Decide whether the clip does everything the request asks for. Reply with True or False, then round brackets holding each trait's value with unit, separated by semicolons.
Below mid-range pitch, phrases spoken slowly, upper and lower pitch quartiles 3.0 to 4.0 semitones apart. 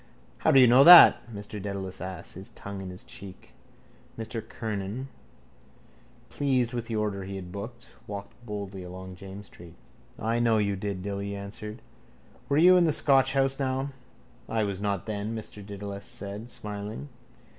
False (105 Hz; 165 wpm; 3.3 semitones)